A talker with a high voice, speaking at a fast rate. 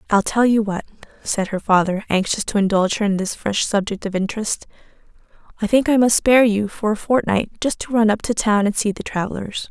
Yes: high, 210 Hz; fast, 220 wpm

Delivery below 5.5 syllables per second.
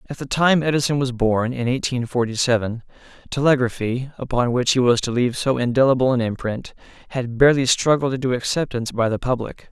No: 5.9 syllables/s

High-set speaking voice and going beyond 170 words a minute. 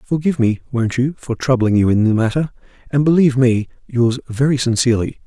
No: low, 125 Hz; average, 180 wpm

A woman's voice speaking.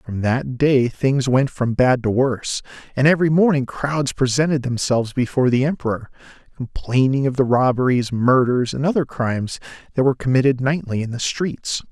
No: male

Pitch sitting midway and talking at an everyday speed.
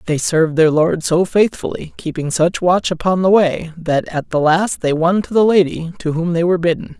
No: medium, 170 Hz; fast, 225 wpm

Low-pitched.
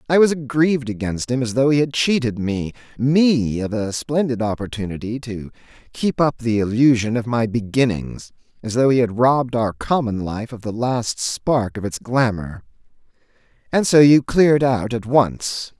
Yes: low, 120 Hz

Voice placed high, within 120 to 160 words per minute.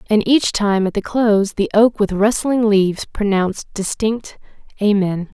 Yes: high, 210 Hz; average, 155 wpm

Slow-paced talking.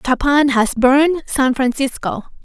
Yes: slow, 125 wpm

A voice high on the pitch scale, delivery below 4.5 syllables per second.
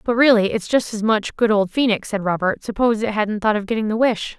No: high, 215 Hz; 5.8 syllables/s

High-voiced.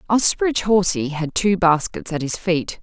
No: medium, 180 Hz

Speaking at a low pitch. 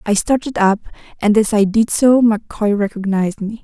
No: high, 215 Hz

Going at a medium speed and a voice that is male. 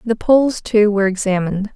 No: average, 170 wpm; female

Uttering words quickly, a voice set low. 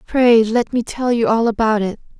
No: fast, 220 wpm; high, 230 Hz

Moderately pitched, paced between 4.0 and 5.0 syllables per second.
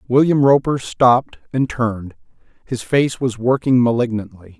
No: low, 125 Hz; 4.7 syllables/s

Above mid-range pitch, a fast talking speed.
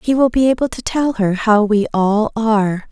Yes: high, 225 Hz; fast, 225 wpm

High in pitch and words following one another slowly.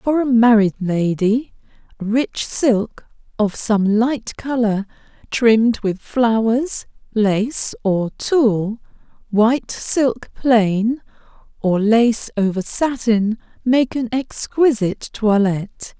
Yes: high, 225 Hz; slow, 100 wpm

